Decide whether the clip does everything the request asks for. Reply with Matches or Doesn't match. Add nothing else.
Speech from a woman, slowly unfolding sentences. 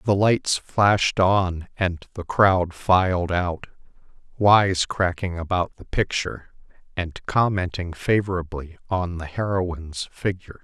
Doesn't match